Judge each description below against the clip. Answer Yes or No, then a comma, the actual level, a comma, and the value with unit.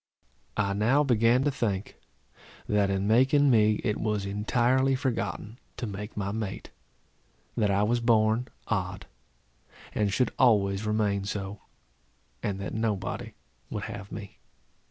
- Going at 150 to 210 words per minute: No, slow, 135 wpm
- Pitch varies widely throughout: No, average, 2.9 semitones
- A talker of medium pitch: No, low, 105 Hz